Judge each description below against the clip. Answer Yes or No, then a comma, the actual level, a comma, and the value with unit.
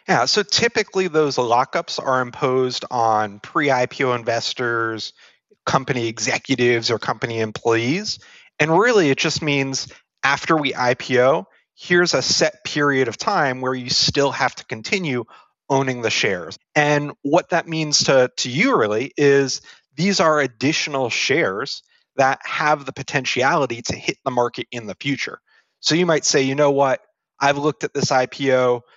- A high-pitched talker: No, low, 135 Hz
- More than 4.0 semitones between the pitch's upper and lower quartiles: No, average, 3.5 semitones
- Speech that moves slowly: No, average, 155 wpm